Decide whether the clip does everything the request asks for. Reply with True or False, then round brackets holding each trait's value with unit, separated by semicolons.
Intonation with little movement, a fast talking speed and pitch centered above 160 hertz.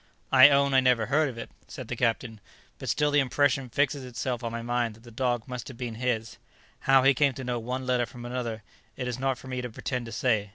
False (2.2 semitones; 250 wpm; 125 Hz)